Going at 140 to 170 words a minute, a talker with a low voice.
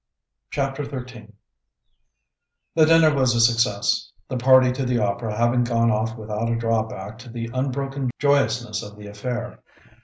Yes: average, 150 wpm; low, 120 Hz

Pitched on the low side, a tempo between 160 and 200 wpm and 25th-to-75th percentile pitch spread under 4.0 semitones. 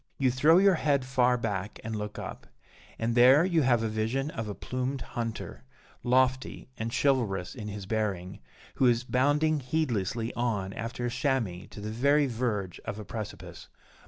Yes: low, 120 Hz; average, 170 wpm; average, 3.6 semitones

